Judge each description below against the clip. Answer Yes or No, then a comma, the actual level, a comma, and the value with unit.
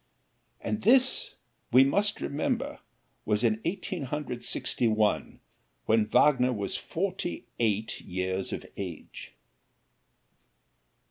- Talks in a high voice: No, low, 125 Hz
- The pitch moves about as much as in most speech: No, wide, 8.3 semitones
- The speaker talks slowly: Yes, slow, 105 wpm